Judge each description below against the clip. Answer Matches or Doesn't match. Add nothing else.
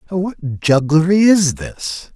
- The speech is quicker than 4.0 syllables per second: Doesn't match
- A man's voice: Matches